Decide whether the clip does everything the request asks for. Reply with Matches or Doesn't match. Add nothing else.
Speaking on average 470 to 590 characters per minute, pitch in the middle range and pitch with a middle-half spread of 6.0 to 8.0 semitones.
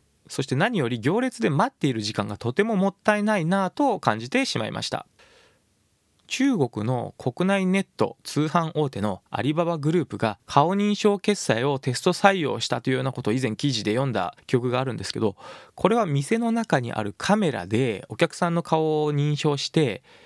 Doesn't match